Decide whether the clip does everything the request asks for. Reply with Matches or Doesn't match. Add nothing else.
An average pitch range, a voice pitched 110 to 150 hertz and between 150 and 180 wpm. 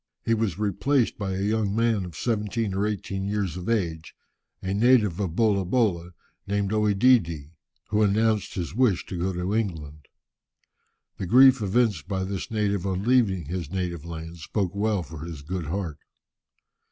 Doesn't match